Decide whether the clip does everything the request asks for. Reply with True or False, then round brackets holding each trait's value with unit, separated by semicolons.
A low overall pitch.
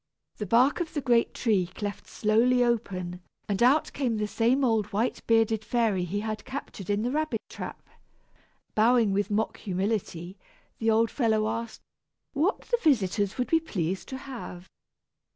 False (225 Hz)